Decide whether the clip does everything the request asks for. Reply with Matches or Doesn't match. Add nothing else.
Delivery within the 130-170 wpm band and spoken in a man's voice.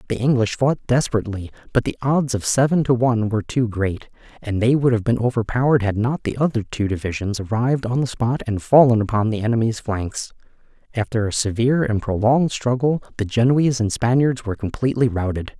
Doesn't match